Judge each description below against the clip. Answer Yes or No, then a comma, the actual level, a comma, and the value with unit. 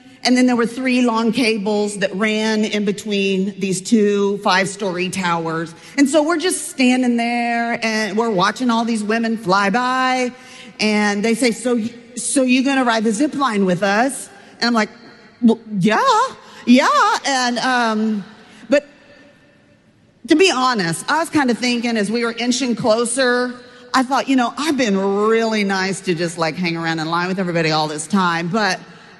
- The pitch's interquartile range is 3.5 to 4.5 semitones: Yes, average, 3.8 semitones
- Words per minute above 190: No, average, 175 wpm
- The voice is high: Yes, high, 225 Hz